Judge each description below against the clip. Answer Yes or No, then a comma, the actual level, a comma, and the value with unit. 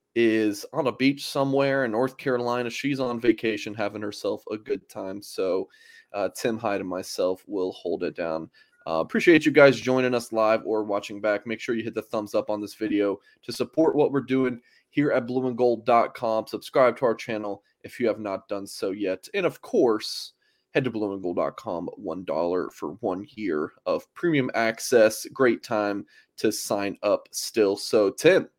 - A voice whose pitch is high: No, low, 120 Hz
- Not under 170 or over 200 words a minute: Yes, average, 180 wpm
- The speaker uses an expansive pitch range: No, average, 4.2 semitones